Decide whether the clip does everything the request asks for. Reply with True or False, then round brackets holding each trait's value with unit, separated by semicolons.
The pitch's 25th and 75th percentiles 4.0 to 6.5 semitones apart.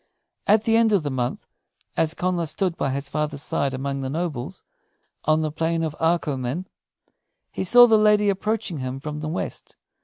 True (5.2 semitones)